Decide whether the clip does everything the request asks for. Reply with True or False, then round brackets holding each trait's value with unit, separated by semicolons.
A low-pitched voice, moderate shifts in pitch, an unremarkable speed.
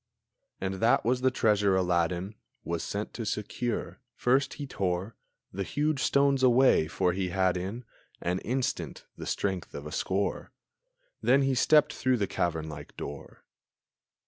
False (100 Hz; 6.1 semitones; 150 wpm)